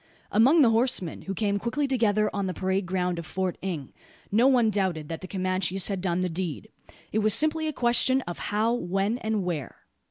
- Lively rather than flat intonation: No, average, 4.1 semitones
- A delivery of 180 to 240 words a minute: Yes, average, 200 wpm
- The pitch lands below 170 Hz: No, high, 200 Hz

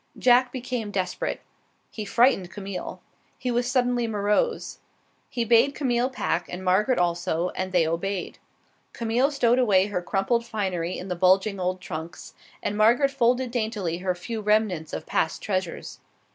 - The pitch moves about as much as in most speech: Yes, average, 4.8 semitones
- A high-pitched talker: Yes, high, 210 Hz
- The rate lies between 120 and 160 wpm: Yes, average, 150 wpm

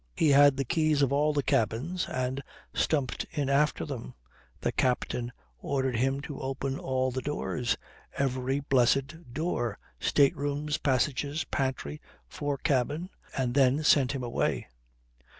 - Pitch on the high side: No, low, 135 Hz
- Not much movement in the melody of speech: Yes, narrow, 2.2 semitones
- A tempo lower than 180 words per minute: Yes, average, 140 wpm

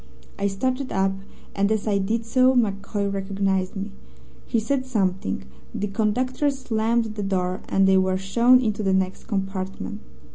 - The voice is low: No, high, 200 Hz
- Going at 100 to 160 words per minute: Yes, average, 155 wpm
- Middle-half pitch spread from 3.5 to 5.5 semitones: No, average, 3.1 semitones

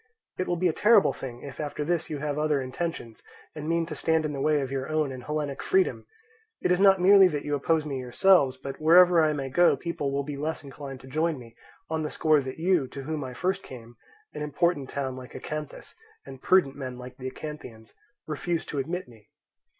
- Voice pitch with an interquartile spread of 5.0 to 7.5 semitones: No, average, 4.0 semitones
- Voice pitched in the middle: Yes, medium, 150 Hz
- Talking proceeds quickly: Yes, fast, 215 wpm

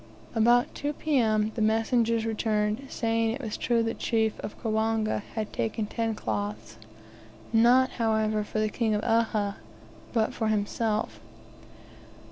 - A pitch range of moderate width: No, narrow, 1.3 semitones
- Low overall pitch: No, high, 220 Hz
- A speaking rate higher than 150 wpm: No, slow, 135 wpm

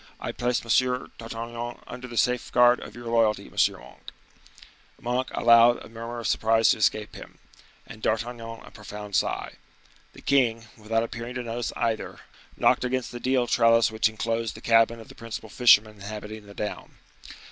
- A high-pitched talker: No, low, 115 Hz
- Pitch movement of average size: No, narrow, 1.6 semitones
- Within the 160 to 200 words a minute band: Yes, average, 170 wpm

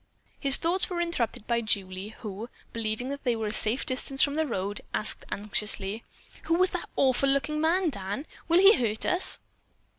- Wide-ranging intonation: Yes, wide, 6.5 semitones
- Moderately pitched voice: No, very high, 250 Hz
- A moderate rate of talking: Yes, average, 180 wpm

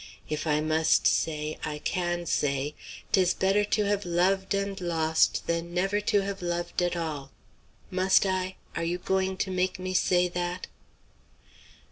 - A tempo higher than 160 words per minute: No, average, 155 wpm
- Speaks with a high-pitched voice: No, medium, 180 Hz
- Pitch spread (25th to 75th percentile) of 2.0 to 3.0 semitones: Yes, narrow, 2.5 semitones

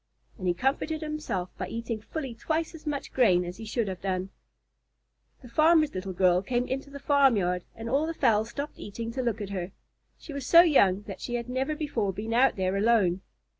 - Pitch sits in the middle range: No, high, 230 Hz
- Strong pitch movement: Yes, wide, 6.6 semitones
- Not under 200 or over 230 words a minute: Yes, fast, 205 wpm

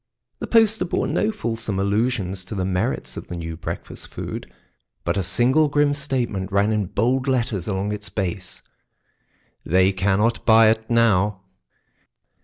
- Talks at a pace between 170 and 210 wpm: No, average, 150 wpm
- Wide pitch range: No, average, 4.3 semitones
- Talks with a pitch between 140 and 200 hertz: No, low, 105 Hz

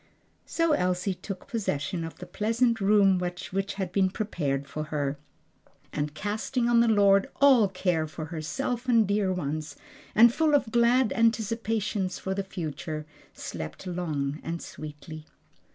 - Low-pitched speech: No, high, 190 Hz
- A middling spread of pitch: No, wide, 6.2 semitones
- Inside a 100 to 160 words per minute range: Yes, average, 145 wpm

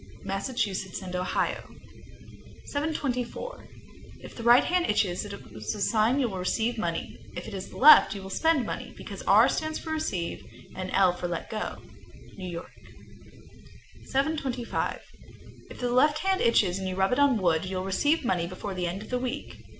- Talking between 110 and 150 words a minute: No, average, 175 wpm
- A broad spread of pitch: Yes, wide, 6.2 semitones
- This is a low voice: No, high, 210 Hz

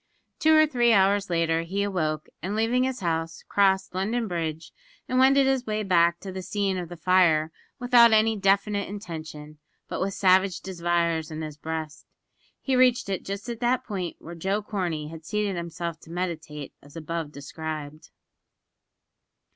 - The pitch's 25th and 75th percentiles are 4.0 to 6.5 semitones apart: Yes, average, 4.4 semitones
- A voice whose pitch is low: No, medium, 185 Hz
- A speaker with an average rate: Yes, average, 165 wpm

